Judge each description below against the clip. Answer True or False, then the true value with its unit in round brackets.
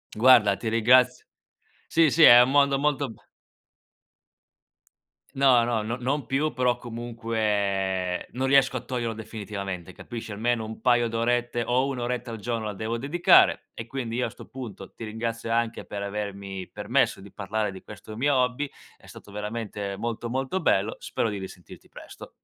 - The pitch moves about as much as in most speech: True (3.2 semitones)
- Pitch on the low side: True (115 Hz)